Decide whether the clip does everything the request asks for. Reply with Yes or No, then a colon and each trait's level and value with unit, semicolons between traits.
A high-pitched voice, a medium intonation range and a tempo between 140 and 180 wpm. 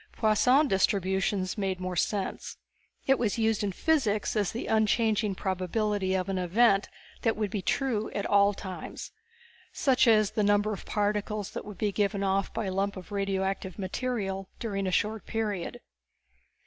No: high, 205 Hz; narrow, 2.2 semitones; average, 160 wpm